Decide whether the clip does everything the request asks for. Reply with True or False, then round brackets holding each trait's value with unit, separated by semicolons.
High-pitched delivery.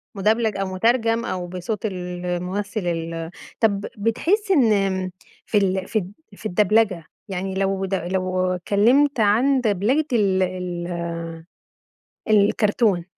True (195 Hz)